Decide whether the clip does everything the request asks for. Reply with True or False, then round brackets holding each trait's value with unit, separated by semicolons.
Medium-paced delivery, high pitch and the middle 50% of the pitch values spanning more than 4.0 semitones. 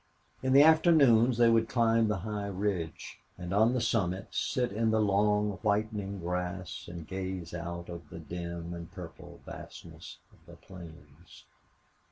False (155 wpm; 100 Hz; 4.5 semitones)